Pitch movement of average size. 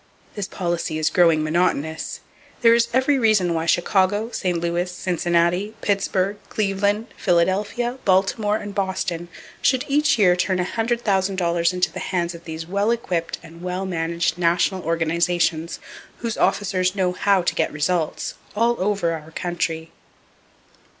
Yes: average, 3.2 semitones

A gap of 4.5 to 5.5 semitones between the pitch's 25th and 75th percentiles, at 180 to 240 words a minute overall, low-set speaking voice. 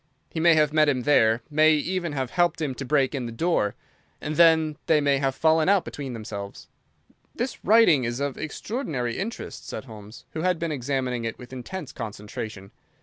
No: average, 4.9 semitones; average, 190 wpm; medium, 145 Hz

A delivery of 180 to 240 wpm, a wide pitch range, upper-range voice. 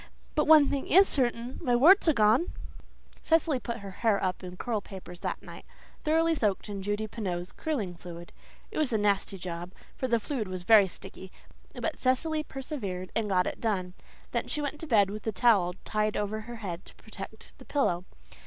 Yes: average, 195 wpm; wide, 5.9 semitones; high, 215 Hz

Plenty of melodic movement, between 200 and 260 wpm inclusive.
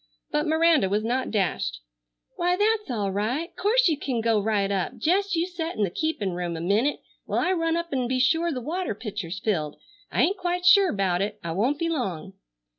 Yes: wide, 9.0 semitones; fast, 205 wpm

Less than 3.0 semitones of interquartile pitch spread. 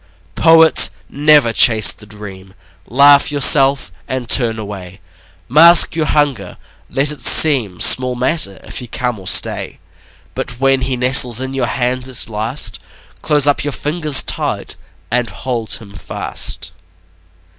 No: average, 4.6 semitones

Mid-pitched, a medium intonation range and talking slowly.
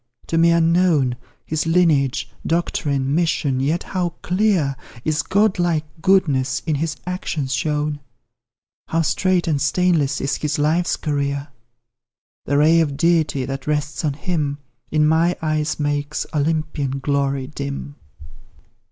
Yes: medium, 150 Hz; average, 3.0 semitones; slow, 130 wpm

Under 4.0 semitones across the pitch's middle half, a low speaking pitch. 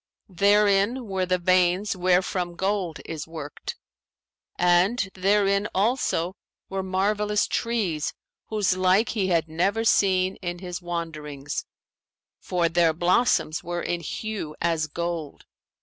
No: average, 2.8 semitones; medium, 185 Hz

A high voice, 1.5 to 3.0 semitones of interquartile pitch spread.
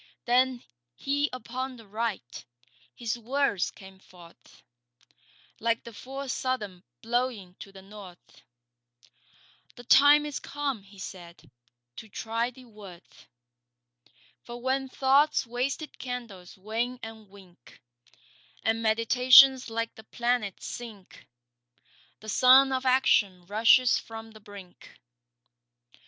No: high, 230 Hz; average, 4.2 semitones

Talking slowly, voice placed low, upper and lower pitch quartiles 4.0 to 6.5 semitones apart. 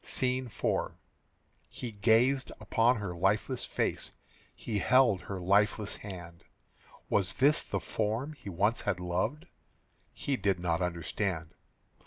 Yes: slow, 125 wpm; low, 105 Hz; average, 5.1 semitones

